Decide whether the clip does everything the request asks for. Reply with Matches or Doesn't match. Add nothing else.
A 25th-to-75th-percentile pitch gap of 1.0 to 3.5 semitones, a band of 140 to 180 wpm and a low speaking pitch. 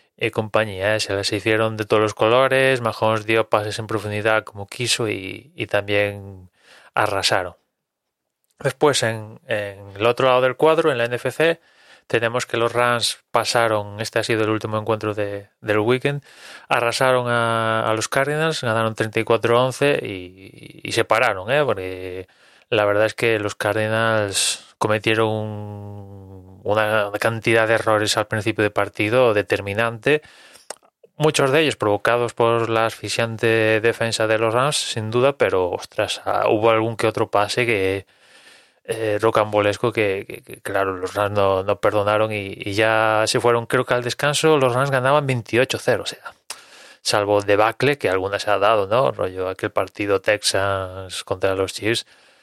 Matches